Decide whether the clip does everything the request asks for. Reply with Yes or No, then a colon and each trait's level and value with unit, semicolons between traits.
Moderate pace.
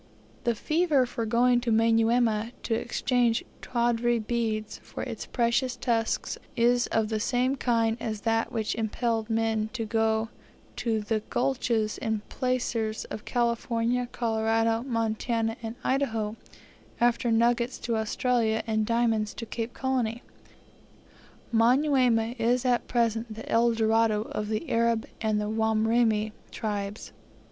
No: slow, 130 wpm